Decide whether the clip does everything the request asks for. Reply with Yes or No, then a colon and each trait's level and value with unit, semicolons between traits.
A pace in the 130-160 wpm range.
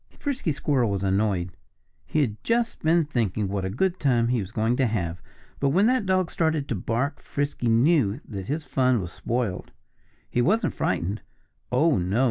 No: average, 180 wpm